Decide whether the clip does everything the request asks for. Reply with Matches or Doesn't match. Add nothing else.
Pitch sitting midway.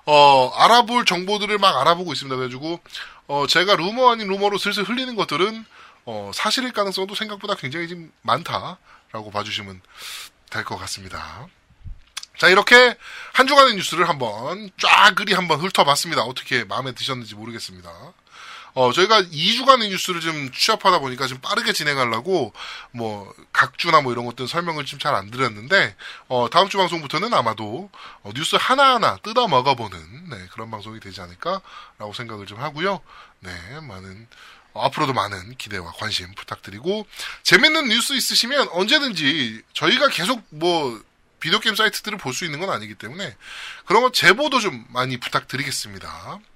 Matches